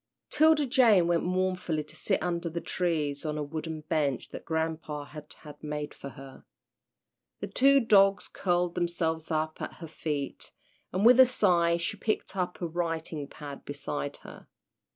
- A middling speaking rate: Yes, average, 165 wpm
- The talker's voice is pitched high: No, medium, 165 Hz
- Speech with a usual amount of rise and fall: Yes, average, 3.4 semitones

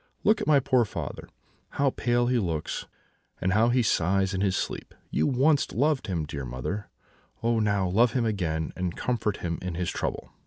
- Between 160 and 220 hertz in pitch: No, low, 100 Hz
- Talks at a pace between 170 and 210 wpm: Yes, average, 190 wpm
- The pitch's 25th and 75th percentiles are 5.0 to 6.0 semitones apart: Yes, wide, 5.4 semitones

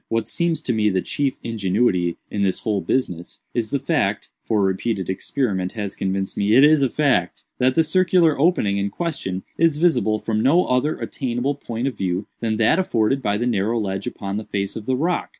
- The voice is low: Yes, low, 115 Hz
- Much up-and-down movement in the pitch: Yes, wide, 5.7 semitones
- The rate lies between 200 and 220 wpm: Yes, fast, 205 wpm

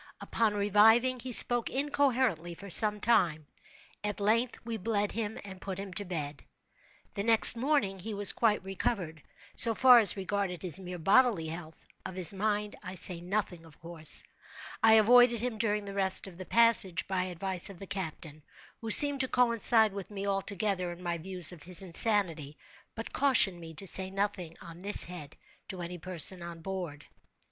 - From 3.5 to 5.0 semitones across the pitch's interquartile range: Yes, average, 4.0 semitones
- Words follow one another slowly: No, average, 180 wpm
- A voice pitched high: Yes, high, 195 Hz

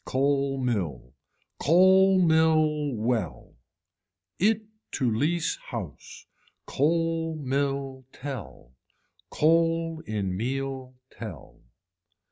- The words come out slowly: Yes, slow, 80 wpm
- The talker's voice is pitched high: No, medium, 140 Hz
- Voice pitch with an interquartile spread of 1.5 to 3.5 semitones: No, average, 5.1 semitones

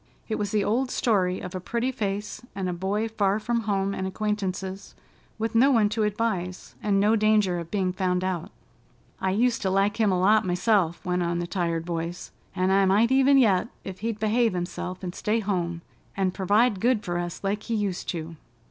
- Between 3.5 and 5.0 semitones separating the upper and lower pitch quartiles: No, average, 3.0 semitones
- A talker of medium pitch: No, high, 195 Hz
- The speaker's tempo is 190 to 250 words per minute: Yes, average, 200 wpm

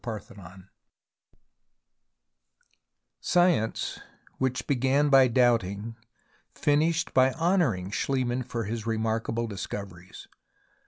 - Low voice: Yes, low, 120 Hz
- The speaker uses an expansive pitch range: No, average, 4.1 semitones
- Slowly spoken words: Yes, slow, 90 wpm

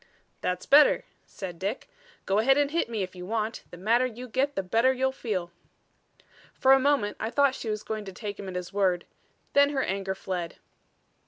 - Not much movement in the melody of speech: No, wide, 5.6 semitones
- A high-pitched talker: Yes, high, 215 Hz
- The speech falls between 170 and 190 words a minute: No, average, 200 wpm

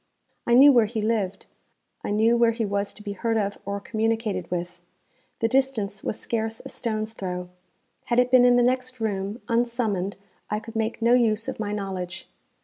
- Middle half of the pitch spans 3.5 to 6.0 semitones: No, average, 2.8 semitones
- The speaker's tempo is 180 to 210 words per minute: Yes, average, 190 wpm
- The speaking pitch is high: Yes, high, 220 Hz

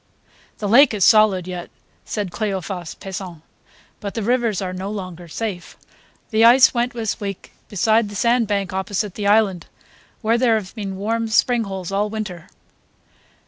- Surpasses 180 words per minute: No, average, 160 wpm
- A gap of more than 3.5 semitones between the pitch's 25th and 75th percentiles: No, average, 2.9 semitones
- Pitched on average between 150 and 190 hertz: No, high, 205 Hz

